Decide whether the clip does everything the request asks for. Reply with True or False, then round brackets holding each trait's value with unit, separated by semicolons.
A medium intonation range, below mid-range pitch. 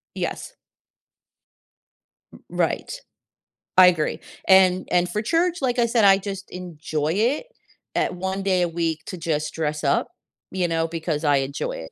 False (3.5 semitones; 180 Hz)